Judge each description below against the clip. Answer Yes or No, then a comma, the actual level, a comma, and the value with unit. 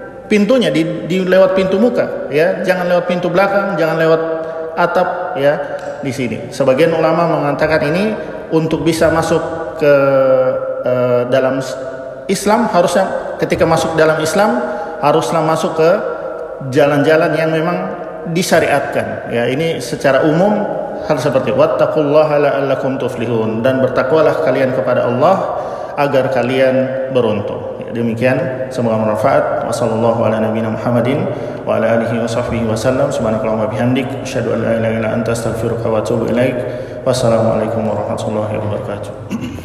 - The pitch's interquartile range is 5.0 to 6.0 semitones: Yes, wide, 5.4 semitones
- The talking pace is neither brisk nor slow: Yes, average, 125 wpm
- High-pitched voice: No, medium, 140 Hz